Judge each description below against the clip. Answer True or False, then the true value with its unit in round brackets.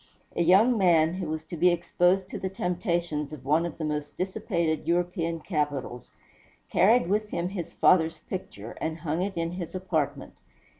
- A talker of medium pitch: True (170 Hz)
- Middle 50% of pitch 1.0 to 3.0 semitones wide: True (2.7 semitones)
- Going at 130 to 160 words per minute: False (170 wpm)